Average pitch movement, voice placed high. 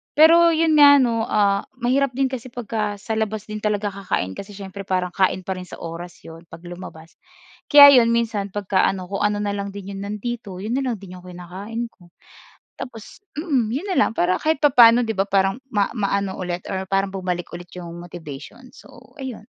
Yes: average, 4.3 semitones; high, 205 Hz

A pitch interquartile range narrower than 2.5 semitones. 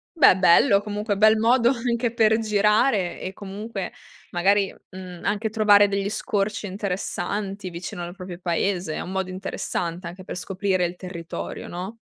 No: average, 2.8 semitones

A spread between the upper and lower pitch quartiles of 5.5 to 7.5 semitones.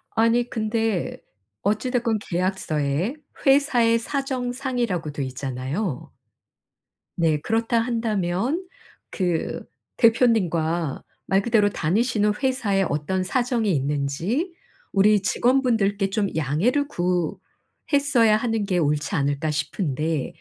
Yes: wide, 6.4 semitones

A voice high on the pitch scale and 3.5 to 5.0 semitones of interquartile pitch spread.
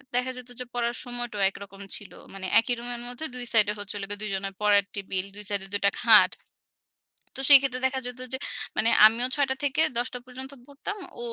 Yes: high, 240 Hz; average, 3.8 semitones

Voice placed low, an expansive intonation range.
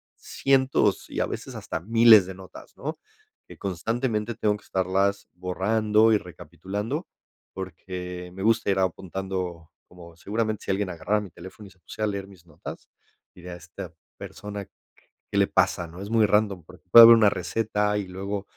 No: low, 100 Hz; average, 2.8 semitones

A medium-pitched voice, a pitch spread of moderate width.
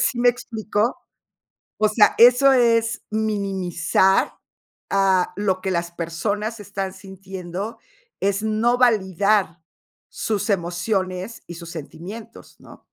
No: high, 200 Hz; average, 3.2 semitones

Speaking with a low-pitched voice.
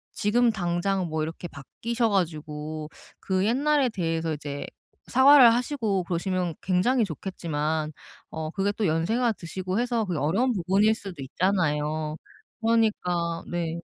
No: medium, 185 Hz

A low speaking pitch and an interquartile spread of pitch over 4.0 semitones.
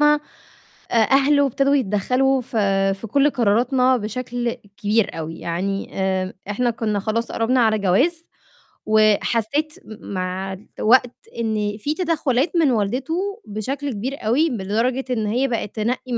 No: high, 235 Hz; average, 4.4 semitones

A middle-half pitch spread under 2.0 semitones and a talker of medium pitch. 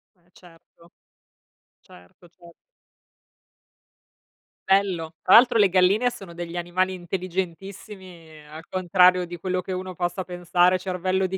Yes: narrow, 1.5 semitones; medium, 180 Hz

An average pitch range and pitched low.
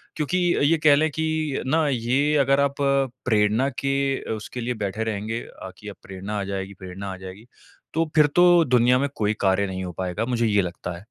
No: wide, 6.1 semitones; low, 120 Hz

